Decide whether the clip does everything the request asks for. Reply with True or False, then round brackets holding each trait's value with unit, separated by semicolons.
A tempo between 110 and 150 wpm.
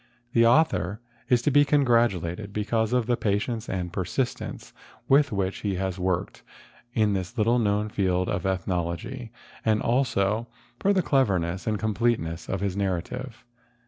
True (145 wpm)